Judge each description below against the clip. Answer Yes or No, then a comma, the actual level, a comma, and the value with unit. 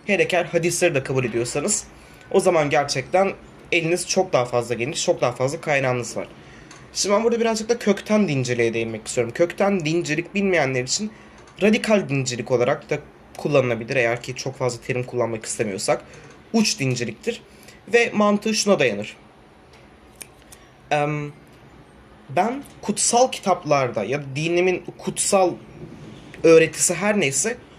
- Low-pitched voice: No, medium, 170 Hz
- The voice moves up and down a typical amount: No, wide, 7.6 semitones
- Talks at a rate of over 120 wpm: Yes, average, 130 wpm